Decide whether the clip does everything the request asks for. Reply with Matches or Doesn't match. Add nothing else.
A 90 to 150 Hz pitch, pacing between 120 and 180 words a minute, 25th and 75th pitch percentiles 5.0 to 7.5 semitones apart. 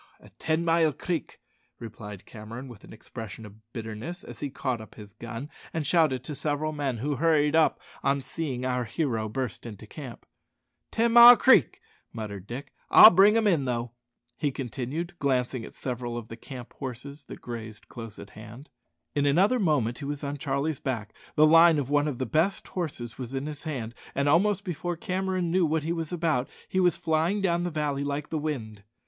Doesn't match